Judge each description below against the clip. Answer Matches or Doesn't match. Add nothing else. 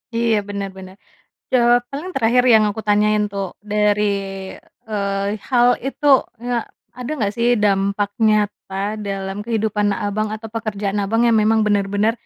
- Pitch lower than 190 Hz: Doesn't match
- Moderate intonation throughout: Doesn't match